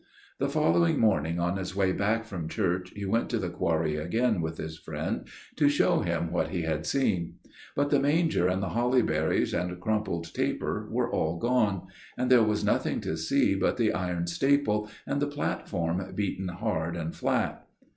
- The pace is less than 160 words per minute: No, average, 185 wpm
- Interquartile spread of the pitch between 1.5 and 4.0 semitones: No, average, 5.0 semitones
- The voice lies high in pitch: No, very low, 95 Hz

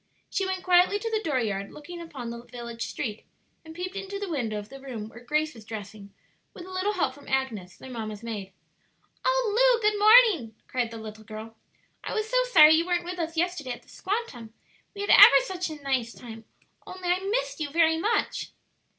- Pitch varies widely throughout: Yes, wide, 8.5 semitones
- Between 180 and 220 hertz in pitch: No, very high, 310 Hz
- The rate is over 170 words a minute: Yes, fast, 205 wpm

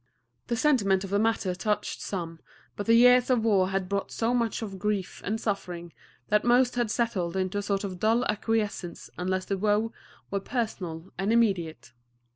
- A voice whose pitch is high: Yes, high, 205 Hz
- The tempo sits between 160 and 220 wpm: Yes, average, 180 wpm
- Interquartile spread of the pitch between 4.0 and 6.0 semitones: No, average, 3.3 semitones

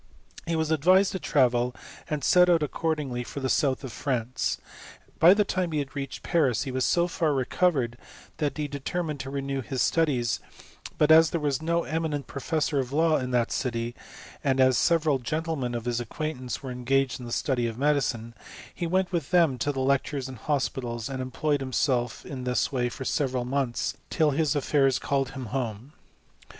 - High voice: No, low, 135 Hz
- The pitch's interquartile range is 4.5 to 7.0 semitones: No, average, 3.8 semitones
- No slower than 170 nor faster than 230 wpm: Yes, average, 185 wpm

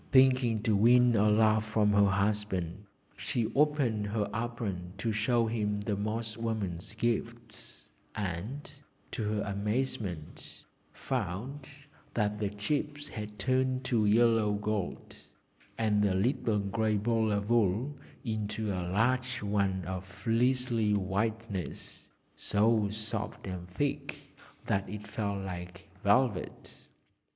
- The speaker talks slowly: Yes, slow, 120 wpm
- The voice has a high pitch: No, low, 105 Hz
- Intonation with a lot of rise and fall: No, narrow, 2.6 semitones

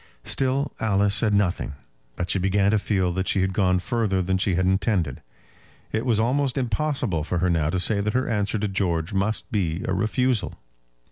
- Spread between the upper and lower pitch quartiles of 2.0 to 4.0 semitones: Yes, average, 3.3 semitones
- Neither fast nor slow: Yes, average, 195 wpm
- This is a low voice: Yes, low, 100 Hz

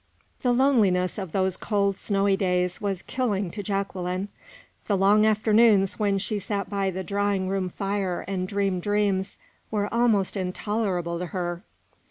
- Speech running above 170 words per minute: No, average, 150 wpm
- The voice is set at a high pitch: Yes, high, 195 Hz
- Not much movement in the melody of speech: Yes, narrow, 1.8 semitones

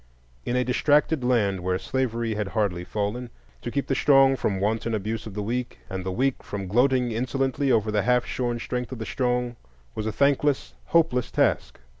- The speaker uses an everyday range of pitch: Yes, average, 3.5 semitones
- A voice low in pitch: Yes, low, 120 Hz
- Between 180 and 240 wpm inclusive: Yes, average, 190 wpm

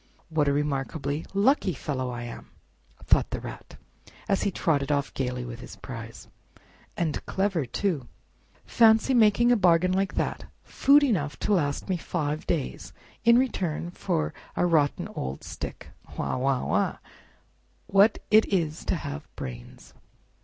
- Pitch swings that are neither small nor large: No, wide, 6.2 semitones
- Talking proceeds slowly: No, average, 145 wpm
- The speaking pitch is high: No, medium, 160 Hz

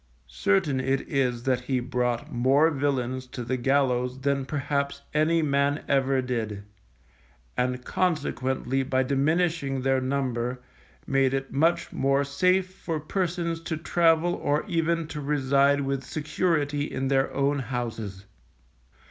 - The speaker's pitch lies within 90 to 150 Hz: Yes, low, 135 Hz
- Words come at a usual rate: No, slow, 130 wpm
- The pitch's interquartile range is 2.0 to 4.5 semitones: Yes, average, 2.8 semitones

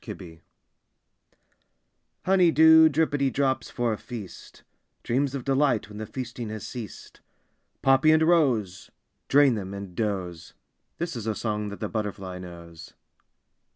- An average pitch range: No, wide, 5.8 semitones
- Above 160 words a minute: No, slow, 135 wpm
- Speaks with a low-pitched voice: Yes, low, 115 Hz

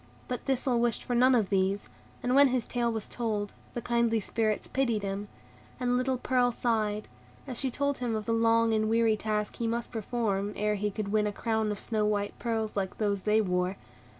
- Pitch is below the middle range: No, high, 225 Hz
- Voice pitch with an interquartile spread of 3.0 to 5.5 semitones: No, narrow, 2.4 semitones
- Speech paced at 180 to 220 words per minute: Yes, fast, 205 wpm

